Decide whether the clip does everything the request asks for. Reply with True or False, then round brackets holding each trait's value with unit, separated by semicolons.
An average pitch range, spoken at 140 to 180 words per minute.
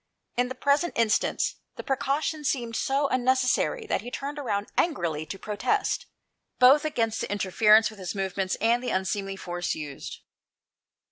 False (5.9 semitones; 150 wpm)